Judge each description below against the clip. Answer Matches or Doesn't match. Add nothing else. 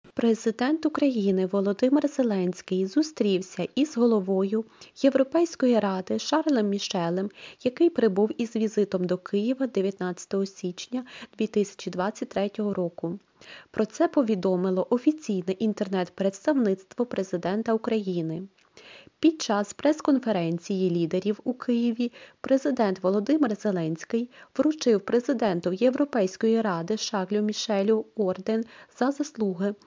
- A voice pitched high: Matches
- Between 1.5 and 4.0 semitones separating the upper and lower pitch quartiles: Doesn't match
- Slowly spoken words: Matches